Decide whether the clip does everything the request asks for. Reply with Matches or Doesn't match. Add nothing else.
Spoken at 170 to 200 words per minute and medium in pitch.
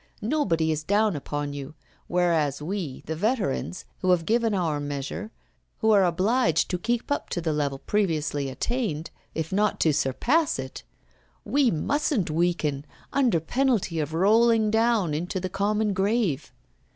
Doesn't match